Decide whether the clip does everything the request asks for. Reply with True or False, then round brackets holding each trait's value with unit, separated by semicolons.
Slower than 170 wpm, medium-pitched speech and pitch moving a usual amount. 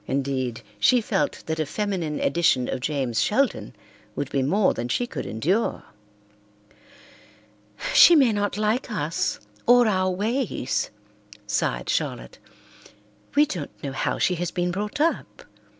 False (135 wpm; 180 Hz; 7.7 semitones)